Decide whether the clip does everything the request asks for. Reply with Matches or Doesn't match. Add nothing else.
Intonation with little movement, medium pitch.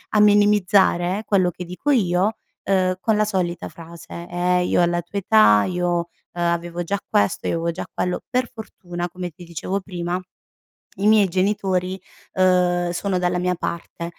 Matches